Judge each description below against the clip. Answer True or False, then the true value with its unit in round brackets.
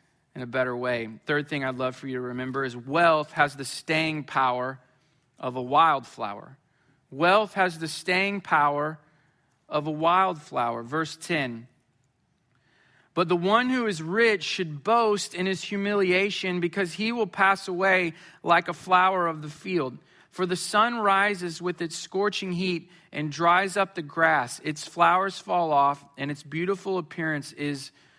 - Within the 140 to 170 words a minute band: True (160 wpm)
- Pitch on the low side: False (165 Hz)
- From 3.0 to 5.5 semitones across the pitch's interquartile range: True (4.5 semitones)